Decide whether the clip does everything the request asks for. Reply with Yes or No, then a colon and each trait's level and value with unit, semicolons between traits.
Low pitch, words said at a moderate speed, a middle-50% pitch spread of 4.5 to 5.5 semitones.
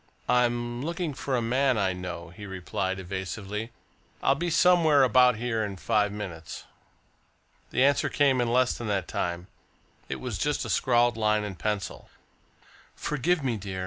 Yes: low, 115 Hz; average, 160 wpm; average, 4.9 semitones